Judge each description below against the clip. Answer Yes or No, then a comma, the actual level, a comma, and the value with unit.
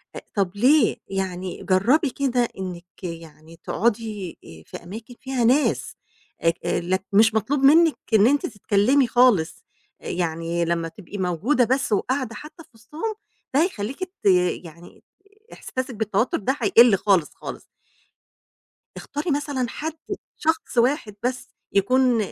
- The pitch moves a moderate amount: No, wide, 6.2 semitones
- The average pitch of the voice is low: No, high, 225 Hz